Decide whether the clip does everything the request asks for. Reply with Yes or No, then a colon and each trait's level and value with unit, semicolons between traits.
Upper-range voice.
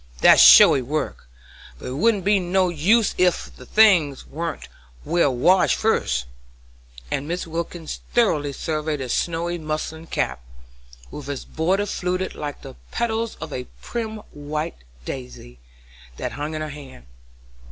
No: medium, 160 Hz